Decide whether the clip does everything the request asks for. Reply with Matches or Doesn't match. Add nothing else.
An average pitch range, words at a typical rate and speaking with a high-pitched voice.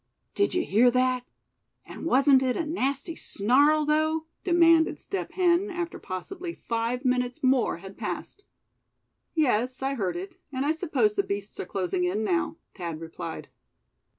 Doesn't match